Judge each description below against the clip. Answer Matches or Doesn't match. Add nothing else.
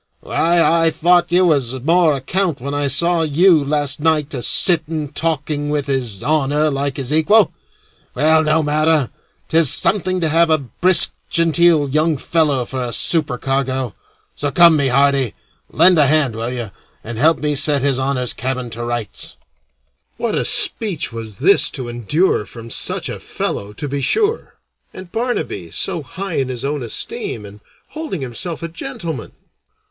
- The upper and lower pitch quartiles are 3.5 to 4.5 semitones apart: Matches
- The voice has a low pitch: Doesn't match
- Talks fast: Doesn't match